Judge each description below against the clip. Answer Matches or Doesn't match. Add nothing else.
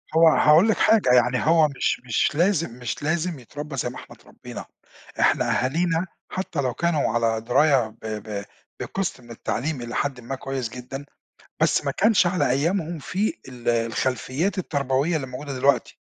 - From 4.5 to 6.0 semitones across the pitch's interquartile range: Matches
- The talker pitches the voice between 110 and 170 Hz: Matches